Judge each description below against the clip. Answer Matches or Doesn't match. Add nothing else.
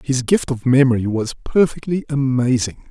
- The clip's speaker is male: Matches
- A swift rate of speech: Doesn't match